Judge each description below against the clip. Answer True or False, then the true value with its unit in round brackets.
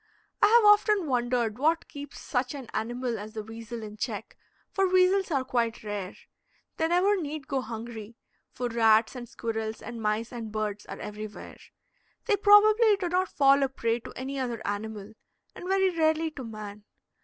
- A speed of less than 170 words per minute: False (175 wpm)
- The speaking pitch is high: True (245 Hz)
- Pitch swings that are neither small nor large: False (6.9 semitones)